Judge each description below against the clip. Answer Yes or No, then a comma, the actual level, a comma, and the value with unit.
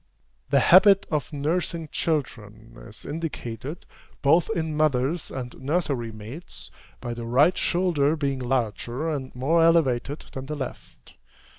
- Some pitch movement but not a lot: Yes, average, 4.7 semitones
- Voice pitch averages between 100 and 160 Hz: Yes, medium, 140 Hz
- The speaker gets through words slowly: Yes, slow, 130 wpm